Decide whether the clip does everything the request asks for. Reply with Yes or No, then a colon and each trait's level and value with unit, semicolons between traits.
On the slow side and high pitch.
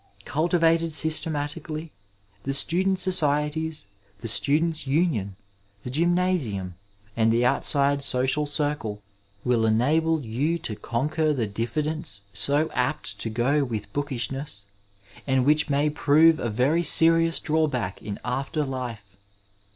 No: slow, 125 wpm; medium, 145 Hz